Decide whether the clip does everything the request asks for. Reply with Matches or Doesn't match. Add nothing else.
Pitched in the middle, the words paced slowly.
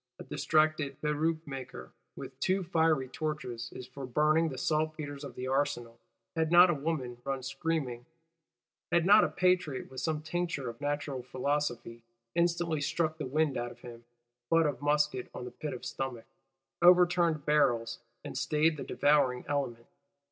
Doesn't match